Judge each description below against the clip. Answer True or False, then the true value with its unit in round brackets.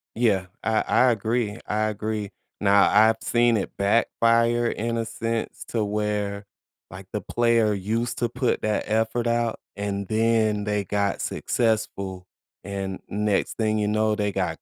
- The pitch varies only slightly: True (2.2 semitones)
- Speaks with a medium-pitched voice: False (110 Hz)